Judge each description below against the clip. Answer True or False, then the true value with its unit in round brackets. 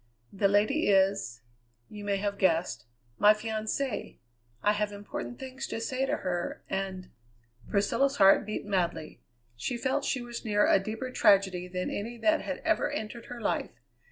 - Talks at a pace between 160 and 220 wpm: True (165 wpm)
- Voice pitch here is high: True (205 Hz)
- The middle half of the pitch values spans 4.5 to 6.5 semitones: False (3.6 semitones)